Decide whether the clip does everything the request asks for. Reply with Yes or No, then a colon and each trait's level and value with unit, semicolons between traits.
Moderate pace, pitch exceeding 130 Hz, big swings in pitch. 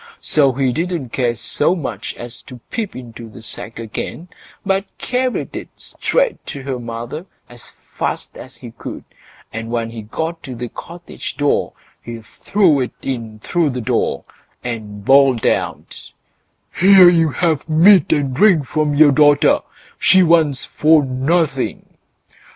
Yes: average, 150 wpm; medium, 140 Hz; wide, 5.8 semitones